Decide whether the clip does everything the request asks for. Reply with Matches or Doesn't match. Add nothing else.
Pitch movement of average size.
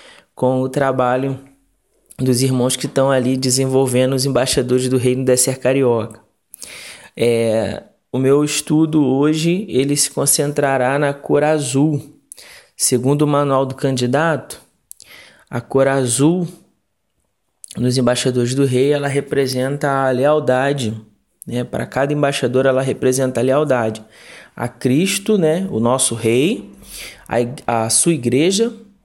Doesn't match